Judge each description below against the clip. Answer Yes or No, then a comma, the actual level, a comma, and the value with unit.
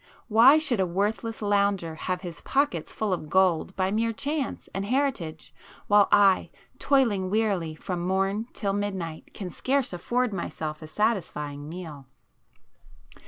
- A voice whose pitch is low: No, high, 195 Hz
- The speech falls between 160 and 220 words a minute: No, average, 140 wpm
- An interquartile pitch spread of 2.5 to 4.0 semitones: No, average, 4.4 semitones